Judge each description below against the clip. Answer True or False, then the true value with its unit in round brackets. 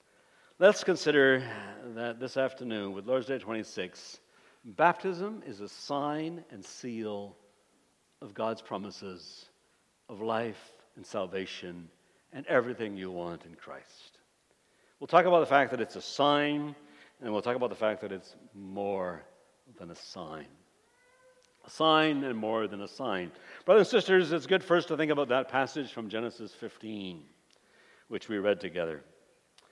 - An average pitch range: False (7.1 semitones)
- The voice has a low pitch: True (125 Hz)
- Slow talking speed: False (150 wpm)